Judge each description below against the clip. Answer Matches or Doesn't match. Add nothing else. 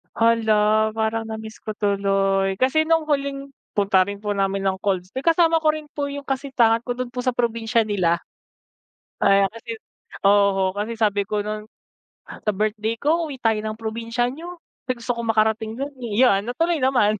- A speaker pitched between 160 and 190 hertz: Doesn't match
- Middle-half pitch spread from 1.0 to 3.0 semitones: Doesn't match